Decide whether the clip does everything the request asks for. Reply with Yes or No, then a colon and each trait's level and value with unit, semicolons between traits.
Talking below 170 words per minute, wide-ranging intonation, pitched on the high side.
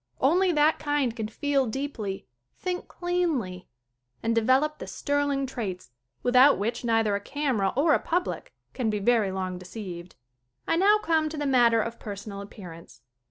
Yes: average, 160 wpm; wide, 6.3 semitones; high, 245 Hz